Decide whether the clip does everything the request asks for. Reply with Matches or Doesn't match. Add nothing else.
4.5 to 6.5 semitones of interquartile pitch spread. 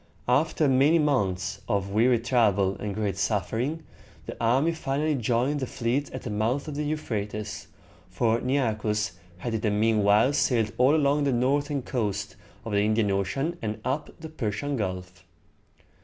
Matches